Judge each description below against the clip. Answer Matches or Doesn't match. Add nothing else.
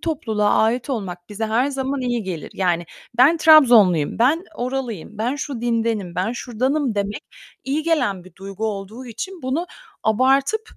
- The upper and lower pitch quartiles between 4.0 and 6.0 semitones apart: Matches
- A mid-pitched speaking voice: Doesn't match